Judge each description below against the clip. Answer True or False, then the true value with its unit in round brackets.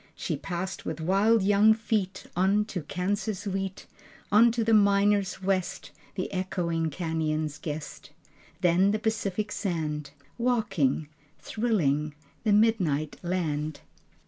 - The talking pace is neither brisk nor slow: False (120 wpm)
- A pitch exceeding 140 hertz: True (190 Hz)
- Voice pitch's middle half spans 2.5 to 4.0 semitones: False (4.5 semitones)